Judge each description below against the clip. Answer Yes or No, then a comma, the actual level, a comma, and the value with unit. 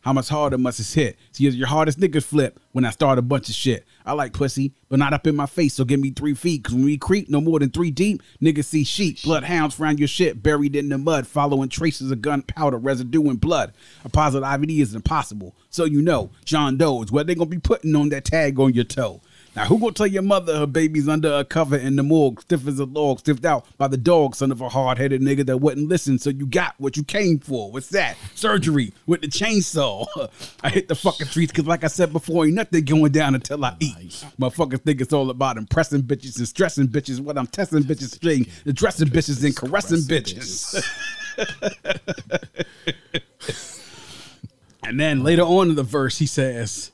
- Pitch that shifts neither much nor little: Yes, average, 3.1 semitones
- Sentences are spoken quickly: Yes, fast, 225 wpm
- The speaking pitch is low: No, medium, 145 Hz